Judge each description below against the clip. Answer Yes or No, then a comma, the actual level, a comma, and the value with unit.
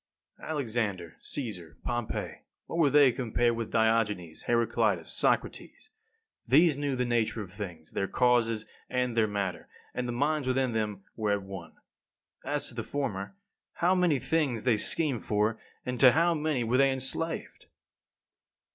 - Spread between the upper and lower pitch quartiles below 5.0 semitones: Yes, average, 4.5 semitones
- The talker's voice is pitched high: No, low, 120 Hz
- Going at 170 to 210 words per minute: No, average, 155 wpm